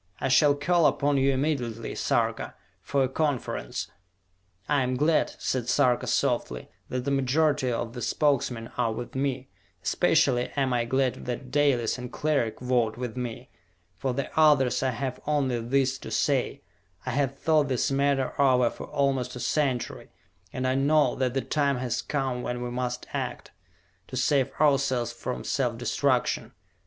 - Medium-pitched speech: No, low, 130 Hz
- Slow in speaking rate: No, average, 165 wpm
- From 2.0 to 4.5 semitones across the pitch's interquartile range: Yes, narrow, 2.4 semitones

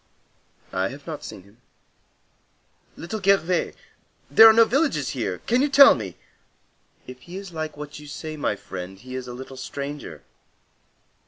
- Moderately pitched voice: Yes, medium, 145 Hz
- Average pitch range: No, wide, 7.3 semitones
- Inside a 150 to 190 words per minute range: Yes, average, 160 wpm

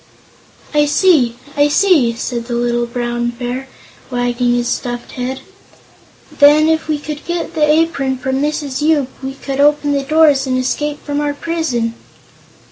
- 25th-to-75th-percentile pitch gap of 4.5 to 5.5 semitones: No, average, 3.5 semitones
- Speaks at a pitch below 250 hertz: No, very high, 275 Hz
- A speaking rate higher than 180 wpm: No, average, 155 wpm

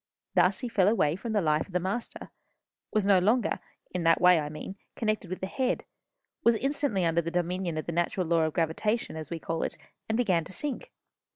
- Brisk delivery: Yes, fast, 215 wpm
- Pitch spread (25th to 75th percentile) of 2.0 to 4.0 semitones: No, average, 4.6 semitones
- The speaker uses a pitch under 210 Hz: Yes, medium, 185 Hz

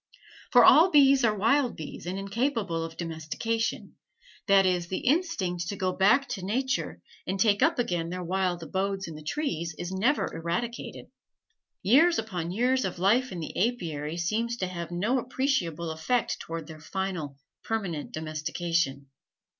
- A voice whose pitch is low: No, high, 190 Hz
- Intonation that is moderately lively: No, wide, 5.9 semitones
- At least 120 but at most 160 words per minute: Yes, average, 155 wpm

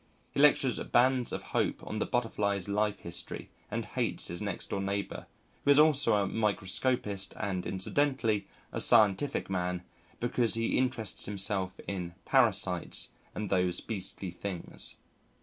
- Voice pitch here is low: Yes, low, 100 Hz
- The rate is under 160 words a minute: Yes, average, 140 wpm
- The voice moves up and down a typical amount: Yes, average, 4.0 semitones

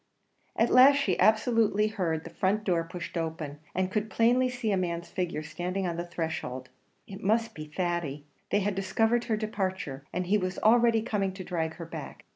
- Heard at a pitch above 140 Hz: Yes, high, 190 Hz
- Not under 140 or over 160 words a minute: No, average, 190 wpm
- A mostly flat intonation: No, average, 4.4 semitones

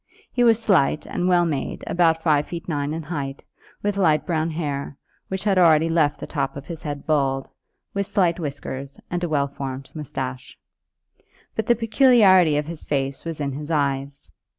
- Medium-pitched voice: Yes, medium, 155 Hz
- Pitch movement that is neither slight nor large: Yes, average, 4.0 semitones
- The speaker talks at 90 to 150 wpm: No, average, 180 wpm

